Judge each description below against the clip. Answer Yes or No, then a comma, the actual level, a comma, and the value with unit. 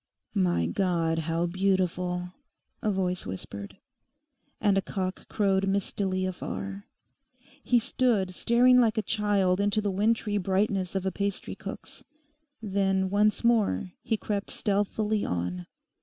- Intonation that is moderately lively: No, narrow, 2.3 semitones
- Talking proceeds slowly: Yes, slow, 125 wpm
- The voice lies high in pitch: Yes, high, 195 Hz